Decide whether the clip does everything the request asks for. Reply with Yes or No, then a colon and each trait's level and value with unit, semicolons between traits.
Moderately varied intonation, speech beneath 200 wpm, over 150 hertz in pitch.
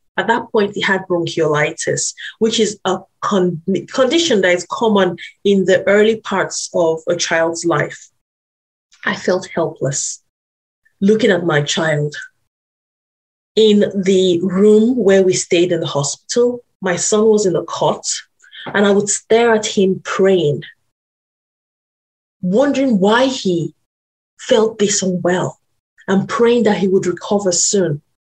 Yes: average, 4.0 semitones; slow, 135 wpm; high, 190 Hz